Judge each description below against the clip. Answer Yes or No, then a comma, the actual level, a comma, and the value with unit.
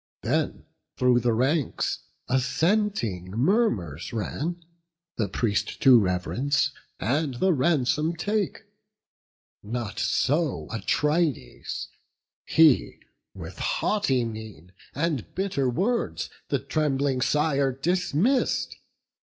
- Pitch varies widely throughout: Yes, wide, 6.1 semitones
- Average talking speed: No, slow, 90 wpm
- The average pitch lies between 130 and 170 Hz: Yes, medium, 140 Hz